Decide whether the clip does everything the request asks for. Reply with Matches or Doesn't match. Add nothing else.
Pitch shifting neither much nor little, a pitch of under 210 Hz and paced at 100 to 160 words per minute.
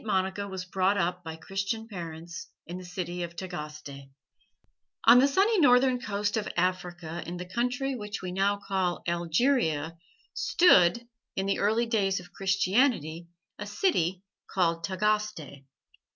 Matches